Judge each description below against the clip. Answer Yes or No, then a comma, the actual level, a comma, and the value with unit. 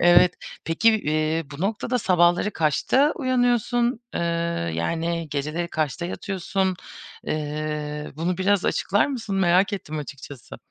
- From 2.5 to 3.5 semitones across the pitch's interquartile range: No, average, 4.8 semitones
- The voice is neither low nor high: Yes, medium, 175 Hz